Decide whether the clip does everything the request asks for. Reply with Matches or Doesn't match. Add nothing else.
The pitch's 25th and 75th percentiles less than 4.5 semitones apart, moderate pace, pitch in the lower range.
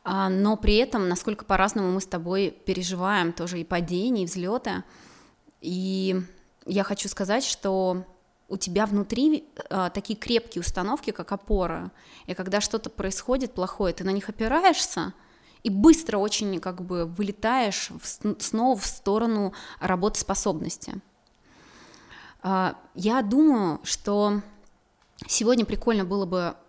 Doesn't match